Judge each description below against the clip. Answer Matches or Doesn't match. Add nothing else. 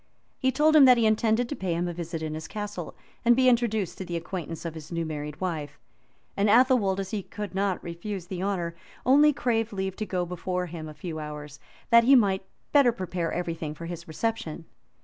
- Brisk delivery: Matches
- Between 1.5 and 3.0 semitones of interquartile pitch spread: Doesn't match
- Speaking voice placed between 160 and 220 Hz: Matches